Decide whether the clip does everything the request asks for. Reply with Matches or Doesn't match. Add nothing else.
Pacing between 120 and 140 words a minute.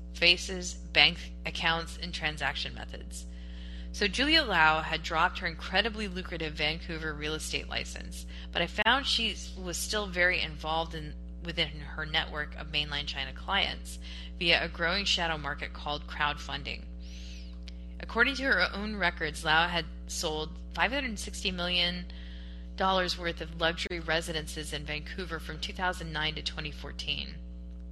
Matches